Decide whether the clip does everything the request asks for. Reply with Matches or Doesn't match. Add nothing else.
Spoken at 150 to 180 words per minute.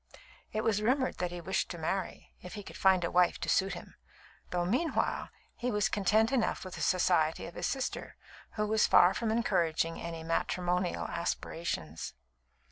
Matches